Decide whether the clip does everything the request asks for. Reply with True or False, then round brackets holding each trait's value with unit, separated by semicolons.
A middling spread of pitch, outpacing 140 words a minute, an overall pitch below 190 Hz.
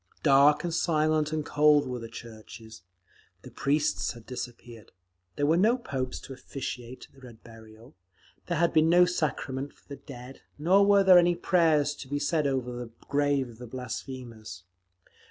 True (4.3 semitones; 170 wpm; 140 Hz)